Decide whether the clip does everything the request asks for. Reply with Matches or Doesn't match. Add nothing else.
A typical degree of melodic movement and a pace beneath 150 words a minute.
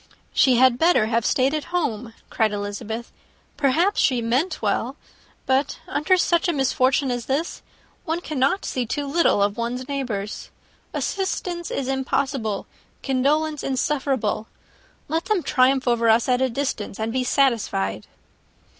Matches